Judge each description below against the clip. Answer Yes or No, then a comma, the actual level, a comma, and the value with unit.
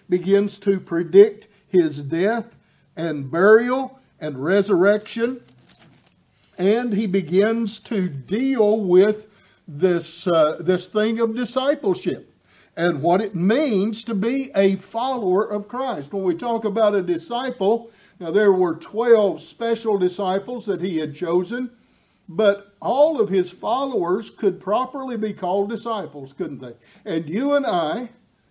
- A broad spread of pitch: No, average, 4.1 semitones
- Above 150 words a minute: No, slow, 135 wpm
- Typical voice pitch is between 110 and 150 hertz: No, high, 205 Hz